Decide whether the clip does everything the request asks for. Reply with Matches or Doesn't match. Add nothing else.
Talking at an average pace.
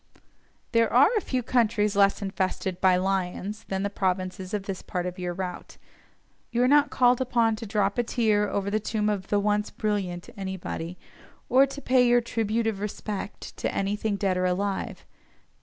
Matches